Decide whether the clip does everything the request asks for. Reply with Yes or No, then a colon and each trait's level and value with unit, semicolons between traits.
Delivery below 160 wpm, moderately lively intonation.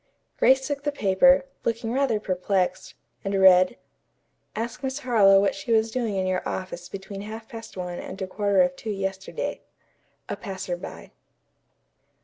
Yes: average, 150 wpm; average, 3.6 semitones